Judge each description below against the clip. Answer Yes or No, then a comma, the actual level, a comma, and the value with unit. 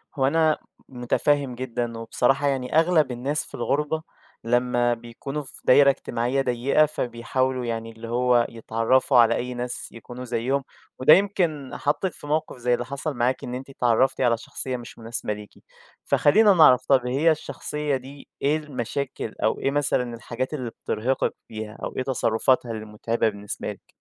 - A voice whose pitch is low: Yes, low, 125 Hz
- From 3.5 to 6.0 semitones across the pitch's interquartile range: No, average, 3.1 semitones